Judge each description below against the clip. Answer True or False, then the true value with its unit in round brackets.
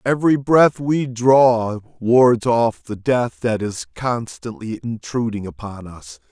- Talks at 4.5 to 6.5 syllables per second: False (3.6 syllables/s)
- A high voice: False (120 Hz)